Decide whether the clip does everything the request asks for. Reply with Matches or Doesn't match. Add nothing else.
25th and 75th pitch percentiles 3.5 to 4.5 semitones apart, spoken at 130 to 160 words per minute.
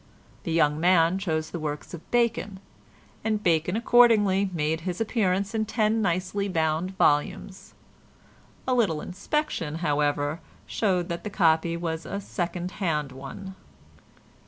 Matches